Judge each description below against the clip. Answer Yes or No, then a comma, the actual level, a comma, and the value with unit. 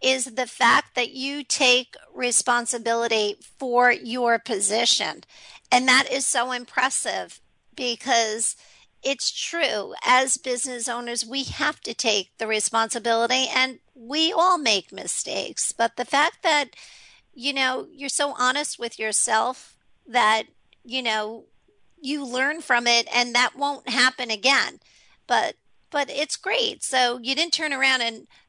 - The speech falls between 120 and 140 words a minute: Yes, slow, 135 wpm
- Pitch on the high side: Yes, very high, 250 Hz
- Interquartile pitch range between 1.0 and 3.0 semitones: Yes, average, 2.7 semitones